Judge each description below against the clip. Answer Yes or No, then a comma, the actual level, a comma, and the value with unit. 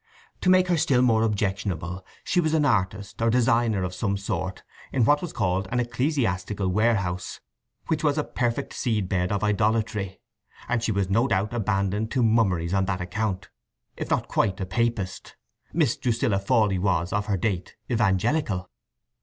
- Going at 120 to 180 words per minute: Yes, average, 165 wpm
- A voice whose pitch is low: Yes, low, 105 Hz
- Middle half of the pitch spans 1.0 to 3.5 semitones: No, average, 4.0 semitones